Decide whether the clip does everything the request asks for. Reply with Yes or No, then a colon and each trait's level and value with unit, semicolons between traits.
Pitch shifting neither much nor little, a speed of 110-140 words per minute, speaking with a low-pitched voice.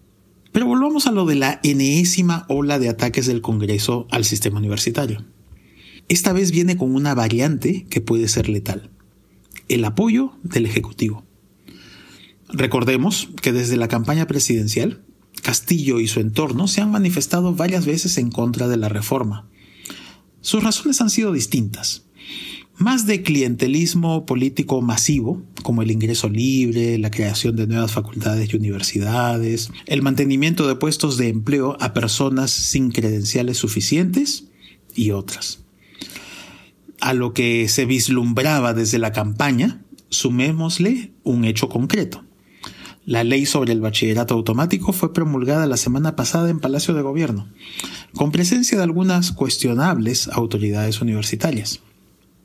No: wide, 5.8 semitones; average, 135 wpm; low, 130 Hz